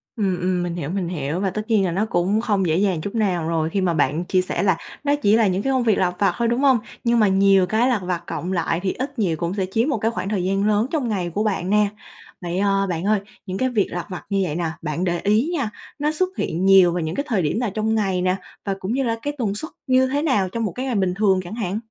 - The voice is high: Yes, high, 195 Hz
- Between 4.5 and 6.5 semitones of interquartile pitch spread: No, average, 3.9 semitones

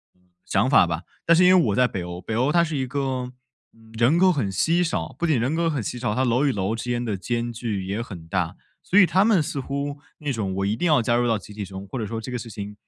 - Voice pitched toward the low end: Yes, low, 120 Hz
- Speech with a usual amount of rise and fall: No, wide, 5.8 semitones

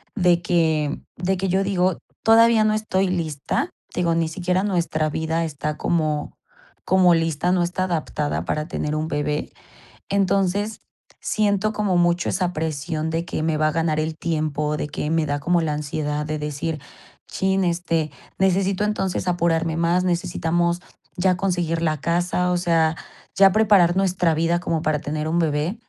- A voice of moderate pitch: Yes, medium, 170 Hz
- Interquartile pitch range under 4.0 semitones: Yes, average, 2.9 semitones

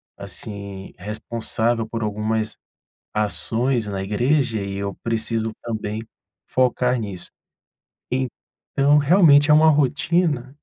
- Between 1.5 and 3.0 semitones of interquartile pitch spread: No, average, 4.1 semitones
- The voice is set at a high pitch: No, low, 115 Hz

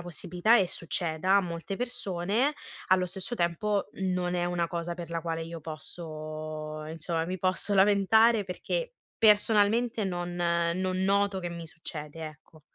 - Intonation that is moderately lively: Yes, average, 3.2 semitones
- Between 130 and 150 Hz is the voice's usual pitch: No, medium, 175 Hz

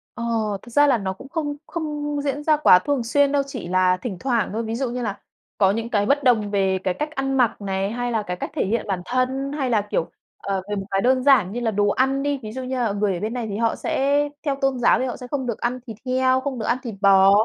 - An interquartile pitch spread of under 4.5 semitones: No, average, 4.8 semitones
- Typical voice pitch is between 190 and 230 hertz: No, high, 240 Hz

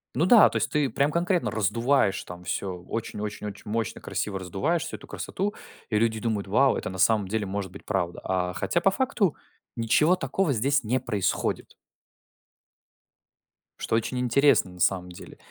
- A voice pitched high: No, low, 110 Hz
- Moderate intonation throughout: No, wide, 6.3 semitones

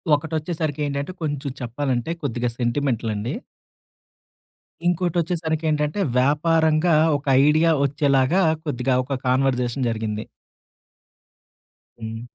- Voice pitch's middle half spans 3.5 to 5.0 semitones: Yes, average, 4.2 semitones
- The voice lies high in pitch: No, medium, 145 Hz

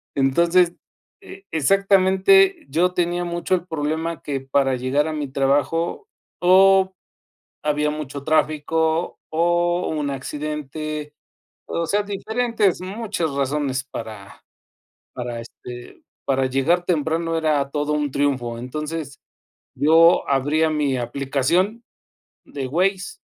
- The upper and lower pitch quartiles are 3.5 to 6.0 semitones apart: Yes, average, 4.2 semitones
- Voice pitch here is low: No, medium, 155 Hz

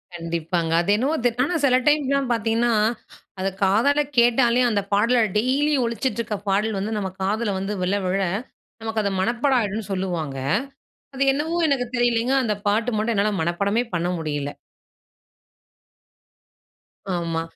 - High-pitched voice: Yes, high, 220 Hz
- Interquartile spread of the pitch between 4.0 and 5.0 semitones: Yes, average, 4.4 semitones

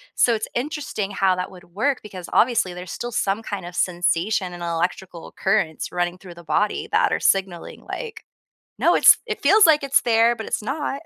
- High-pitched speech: Yes, high, 200 Hz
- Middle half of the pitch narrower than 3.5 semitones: No, average, 5.3 semitones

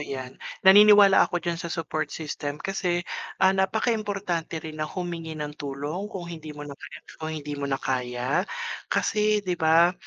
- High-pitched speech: No, medium, 165 Hz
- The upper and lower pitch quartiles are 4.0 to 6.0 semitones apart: Yes, average, 4.4 semitones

